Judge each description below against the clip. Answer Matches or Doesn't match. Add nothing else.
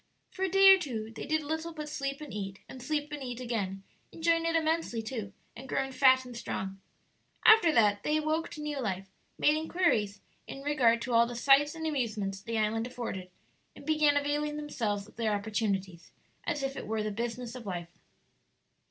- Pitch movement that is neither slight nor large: Doesn't match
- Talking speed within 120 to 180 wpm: Doesn't match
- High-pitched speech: Matches